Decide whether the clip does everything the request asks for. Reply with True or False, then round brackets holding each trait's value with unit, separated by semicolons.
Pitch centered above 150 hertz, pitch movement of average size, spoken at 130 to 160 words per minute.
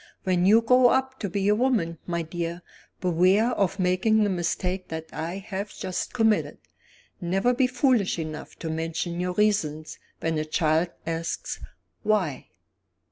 True (185 Hz; 4.4 semitones; 150 wpm)